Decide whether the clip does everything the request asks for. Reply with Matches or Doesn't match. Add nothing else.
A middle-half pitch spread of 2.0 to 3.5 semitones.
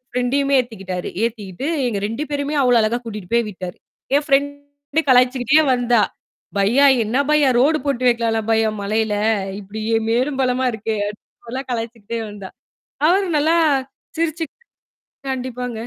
Doesn't match